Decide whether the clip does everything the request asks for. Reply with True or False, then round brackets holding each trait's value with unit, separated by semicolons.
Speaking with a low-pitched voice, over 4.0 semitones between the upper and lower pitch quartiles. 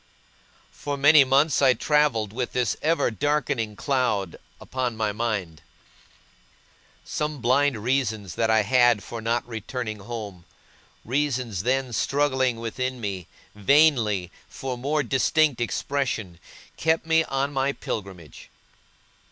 True (125 Hz; 4.4 semitones)